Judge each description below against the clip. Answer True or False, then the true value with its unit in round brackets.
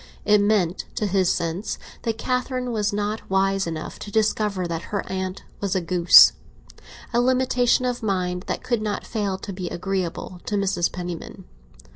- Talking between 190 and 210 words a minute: False (160 wpm)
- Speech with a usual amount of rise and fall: True (3.1 semitones)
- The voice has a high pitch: True (195 Hz)